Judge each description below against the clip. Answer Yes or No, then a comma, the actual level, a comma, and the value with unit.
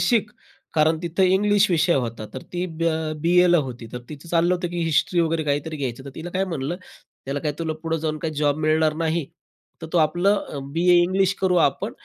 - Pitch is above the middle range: No, medium, 165 Hz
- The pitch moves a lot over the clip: No, average, 2.8 semitones